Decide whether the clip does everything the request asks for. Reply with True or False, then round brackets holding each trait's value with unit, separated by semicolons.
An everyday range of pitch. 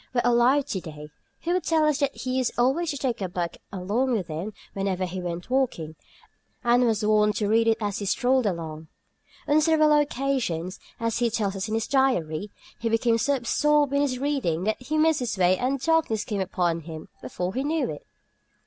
False (6.6 semitones)